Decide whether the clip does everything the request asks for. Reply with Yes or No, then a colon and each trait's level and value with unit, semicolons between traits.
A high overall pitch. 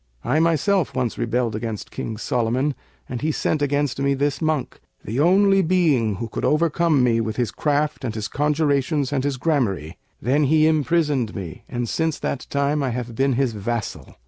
No: medium, 140 Hz